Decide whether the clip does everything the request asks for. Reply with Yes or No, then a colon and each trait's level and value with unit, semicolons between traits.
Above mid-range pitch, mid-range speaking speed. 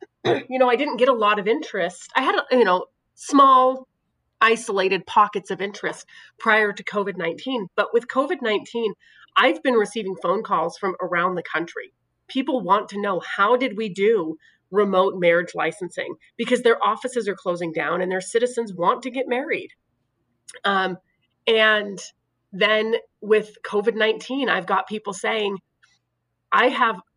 Yes: high, 215 Hz; average, 155 wpm